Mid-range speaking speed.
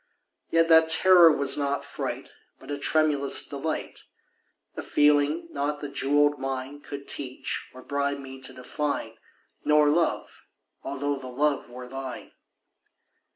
No: slow, 130 wpm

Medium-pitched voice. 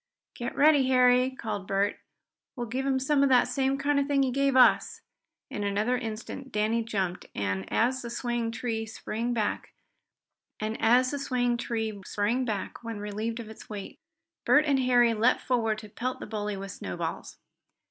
No: high, 235 Hz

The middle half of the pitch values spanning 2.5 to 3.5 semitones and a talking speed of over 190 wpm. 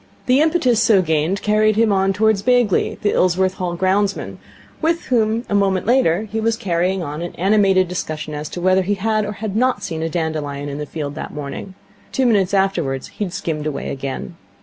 No: average, 4.8 semitones; fast, 205 wpm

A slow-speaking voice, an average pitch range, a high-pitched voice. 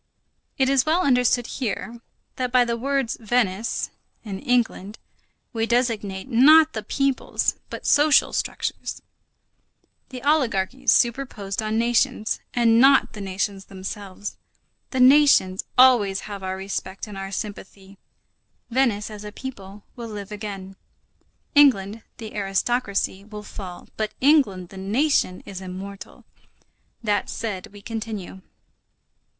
Yes: slow, 120 wpm; average, 4.2 semitones; high, 215 Hz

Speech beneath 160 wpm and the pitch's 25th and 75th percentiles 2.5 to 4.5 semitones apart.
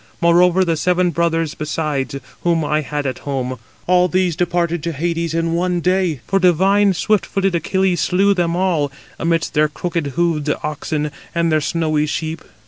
No: average, 170 wpm; average, 2.8 semitones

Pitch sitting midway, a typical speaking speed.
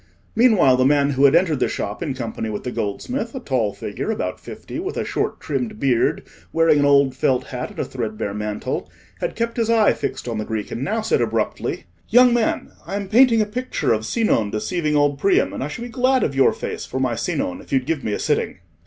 No: medium, 145 Hz; fast, 225 wpm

